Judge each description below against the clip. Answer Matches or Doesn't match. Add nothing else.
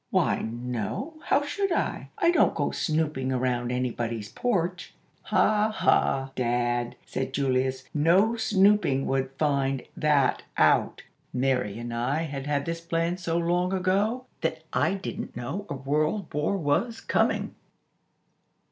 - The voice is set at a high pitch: Doesn't match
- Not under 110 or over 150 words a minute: Matches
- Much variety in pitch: Matches